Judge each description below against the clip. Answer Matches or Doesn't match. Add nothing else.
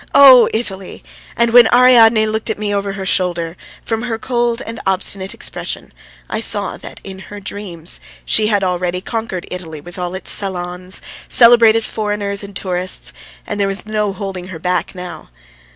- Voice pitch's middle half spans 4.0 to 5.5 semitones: Doesn't match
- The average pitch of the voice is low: Doesn't match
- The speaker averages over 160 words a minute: Matches